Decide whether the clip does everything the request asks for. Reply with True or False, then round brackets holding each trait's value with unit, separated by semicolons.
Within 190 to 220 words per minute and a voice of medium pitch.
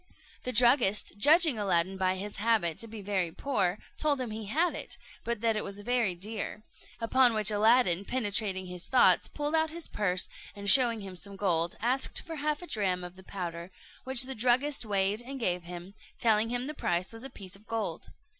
False (200 wpm; 215 Hz)